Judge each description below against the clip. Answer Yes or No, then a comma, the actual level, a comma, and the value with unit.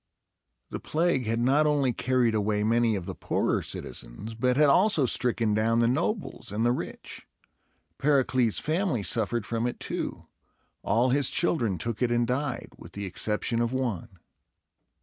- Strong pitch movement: No, average, 3.2 semitones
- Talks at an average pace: Yes, average, 160 wpm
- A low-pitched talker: Yes, low, 120 Hz